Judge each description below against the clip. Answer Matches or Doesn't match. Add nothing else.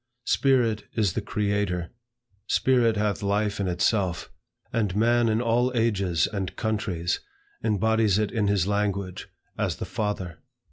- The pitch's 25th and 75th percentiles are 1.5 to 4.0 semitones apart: Matches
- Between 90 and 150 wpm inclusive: Matches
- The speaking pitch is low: Matches